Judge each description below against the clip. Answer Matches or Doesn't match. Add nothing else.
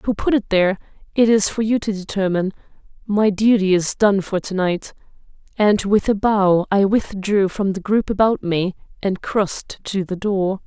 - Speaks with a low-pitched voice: Doesn't match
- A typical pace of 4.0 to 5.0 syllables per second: Matches